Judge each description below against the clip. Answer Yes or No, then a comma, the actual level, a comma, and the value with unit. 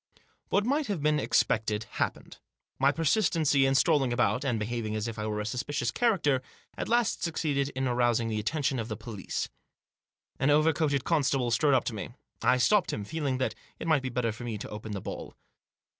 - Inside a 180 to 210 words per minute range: Yes, average, 200 wpm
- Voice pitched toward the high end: No, low, 130 Hz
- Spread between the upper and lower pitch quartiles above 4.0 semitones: Yes, average, 5.0 semitones